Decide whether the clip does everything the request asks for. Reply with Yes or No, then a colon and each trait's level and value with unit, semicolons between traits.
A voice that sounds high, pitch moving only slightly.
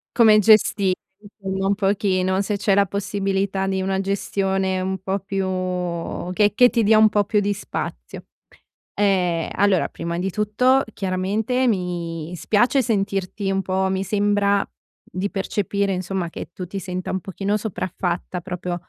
Yes: high, 195 Hz; narrow, 1.7 semitones